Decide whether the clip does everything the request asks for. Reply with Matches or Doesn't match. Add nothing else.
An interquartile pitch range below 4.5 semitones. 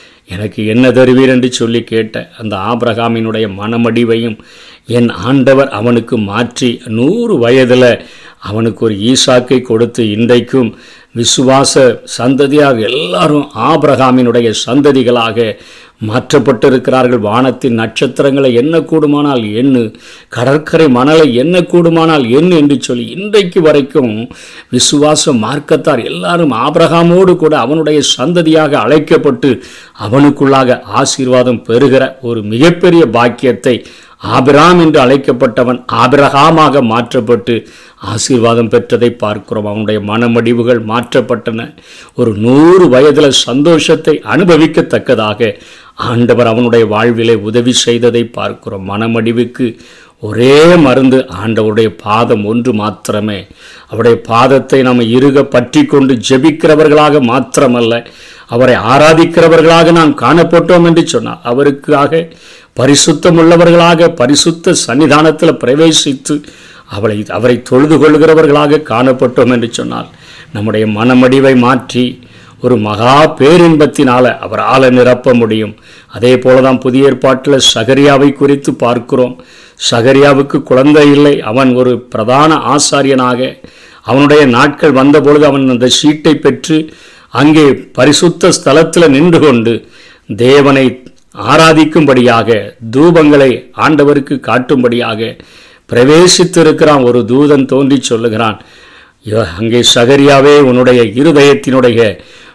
Matches